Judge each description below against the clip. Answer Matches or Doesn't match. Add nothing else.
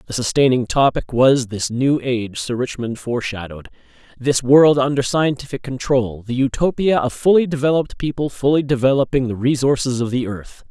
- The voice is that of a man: Matches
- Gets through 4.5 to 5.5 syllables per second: Matches